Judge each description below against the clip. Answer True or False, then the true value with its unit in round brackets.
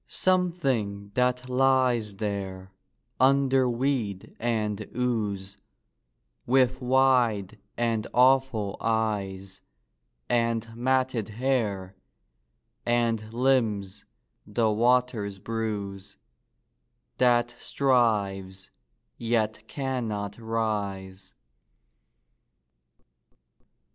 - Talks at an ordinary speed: False (70 wpm)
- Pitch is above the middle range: False (115 Hz)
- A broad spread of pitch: False (3.8 semitones)